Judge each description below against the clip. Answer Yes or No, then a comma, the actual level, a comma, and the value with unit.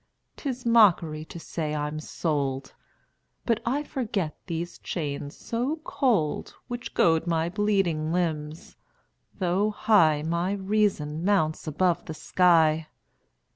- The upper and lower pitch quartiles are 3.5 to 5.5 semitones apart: Yes, average, 5.0 semitones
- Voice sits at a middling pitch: Yes, medium, 170 Hz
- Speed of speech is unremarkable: No, slow, 115 wpm